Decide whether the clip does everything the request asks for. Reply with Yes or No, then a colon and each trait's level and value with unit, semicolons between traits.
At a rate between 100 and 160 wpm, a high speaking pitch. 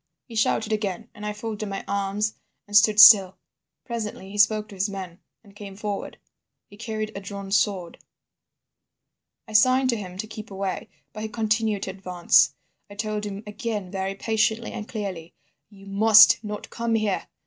No: average, 170 wpm; high, 210 Hz